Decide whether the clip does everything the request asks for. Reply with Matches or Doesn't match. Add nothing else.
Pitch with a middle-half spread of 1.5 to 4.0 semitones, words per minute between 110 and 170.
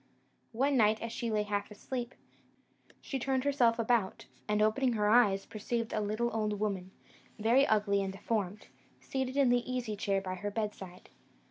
Matches